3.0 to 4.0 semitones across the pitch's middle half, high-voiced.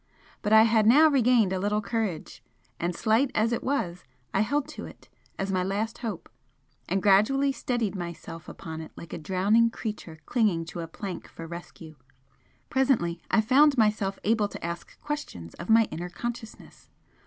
No: average, 4.8 semitones; high, 210 Hz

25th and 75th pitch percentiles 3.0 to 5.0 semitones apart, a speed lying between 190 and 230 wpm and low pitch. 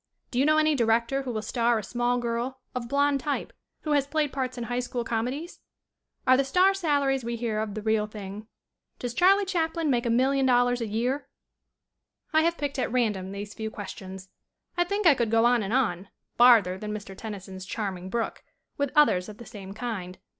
No: average, 4.4 semitones; average, 200 wpm; high, 240 Hz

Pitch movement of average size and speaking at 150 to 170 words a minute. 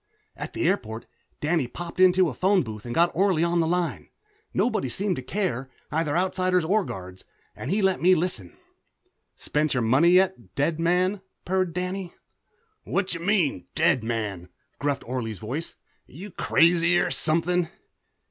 No: wide, 6.0 semitones; average, 155 wpm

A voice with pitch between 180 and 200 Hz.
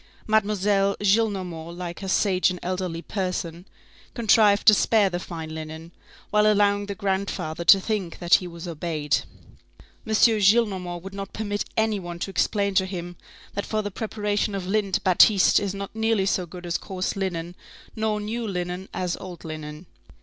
Yes: high, 190 Hz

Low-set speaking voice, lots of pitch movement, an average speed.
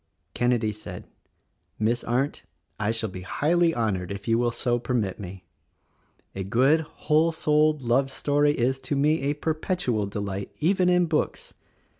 Yes: low, 125 Hz; wide, 5.9 semitones; average, 150 wpm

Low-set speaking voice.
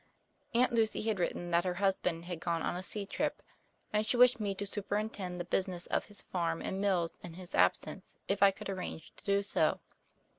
No: high, 190 Hz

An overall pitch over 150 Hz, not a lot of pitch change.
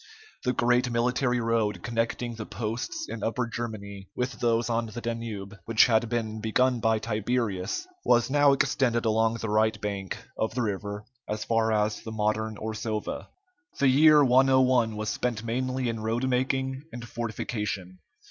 No: low, 115 Hz; narrow, 2.3 semitones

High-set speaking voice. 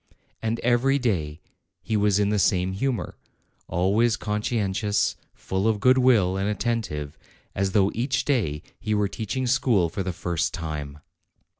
No: low, 105 Hz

